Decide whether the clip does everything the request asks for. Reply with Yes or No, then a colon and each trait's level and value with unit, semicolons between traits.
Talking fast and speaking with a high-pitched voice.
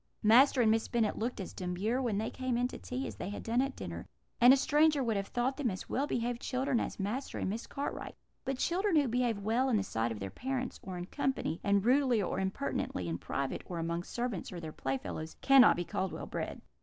Yes: fast, 235 wpm; high, 230 Hz